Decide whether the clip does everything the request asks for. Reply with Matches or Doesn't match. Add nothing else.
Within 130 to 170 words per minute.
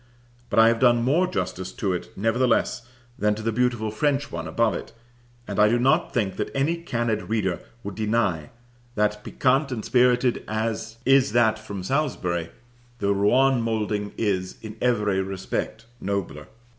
Matches